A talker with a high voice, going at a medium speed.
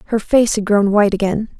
No: high, 210 Hz; fast, 225 wpm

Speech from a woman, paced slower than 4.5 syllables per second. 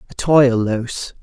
No: male; 4.1 syllables/s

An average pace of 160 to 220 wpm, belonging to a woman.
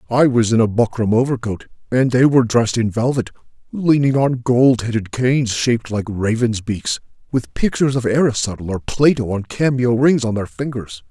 No: average, 180 wpm; male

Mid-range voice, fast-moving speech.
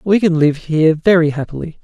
No: medium, 165 Hz; average, 195 wpm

